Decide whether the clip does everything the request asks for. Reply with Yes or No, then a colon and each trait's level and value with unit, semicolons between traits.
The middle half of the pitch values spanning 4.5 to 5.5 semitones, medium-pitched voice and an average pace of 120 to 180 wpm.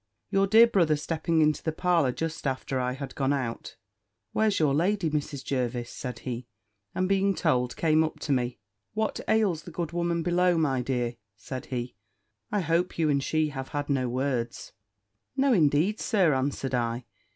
Yes: average, 5.1 semitones; medium, 150 Hz; average, 175 wpm